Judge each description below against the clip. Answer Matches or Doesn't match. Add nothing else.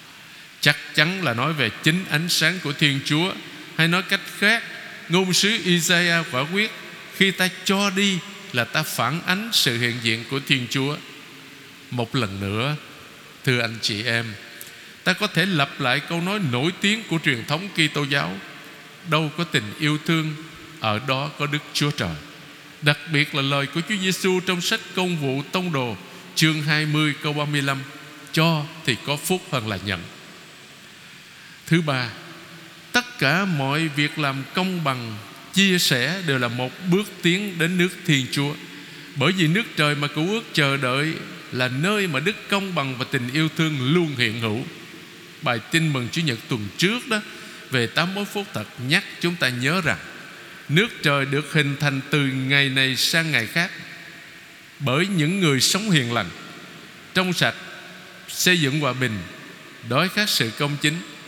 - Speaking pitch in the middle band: Matches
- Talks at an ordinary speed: Matches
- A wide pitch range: Doesn't match